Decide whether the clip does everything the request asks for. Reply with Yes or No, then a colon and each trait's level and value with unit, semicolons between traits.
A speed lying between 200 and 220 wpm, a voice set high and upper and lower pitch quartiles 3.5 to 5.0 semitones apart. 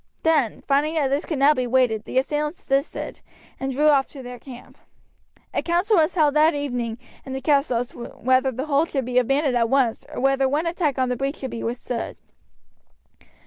No: fast, 205 wpm; very high, 270 Hz; average, 3.1 semitones